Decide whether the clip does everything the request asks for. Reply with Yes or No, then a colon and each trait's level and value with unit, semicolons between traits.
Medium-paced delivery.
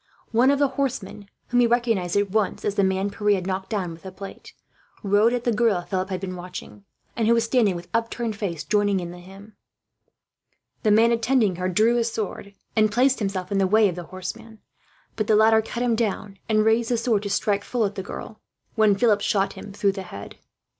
No: fast, 220 wpm